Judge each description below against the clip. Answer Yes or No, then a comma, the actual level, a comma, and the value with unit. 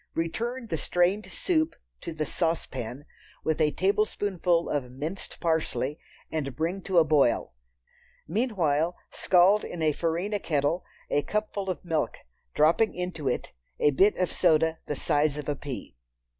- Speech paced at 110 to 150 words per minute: Yes, average, 145 wpm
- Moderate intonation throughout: Yes, average, 4.2 semitones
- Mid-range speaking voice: Yes, medium, 165 Hz